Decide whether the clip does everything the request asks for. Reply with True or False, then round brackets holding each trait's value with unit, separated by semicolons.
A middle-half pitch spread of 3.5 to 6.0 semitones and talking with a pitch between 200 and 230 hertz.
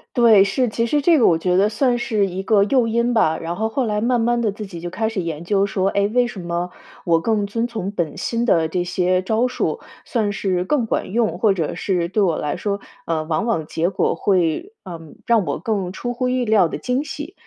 True (4.8 semitones; 205 Hz)